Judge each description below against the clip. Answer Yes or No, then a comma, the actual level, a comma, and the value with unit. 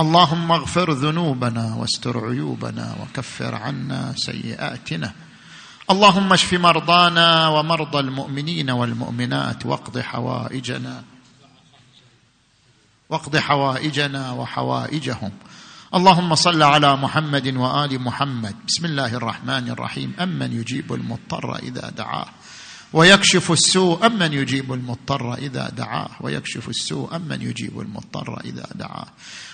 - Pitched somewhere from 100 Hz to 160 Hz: Yes, medium, 140 Hz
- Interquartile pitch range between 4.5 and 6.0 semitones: Yes, average, 5.2 semitones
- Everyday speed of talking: Yes, average, 100 wpm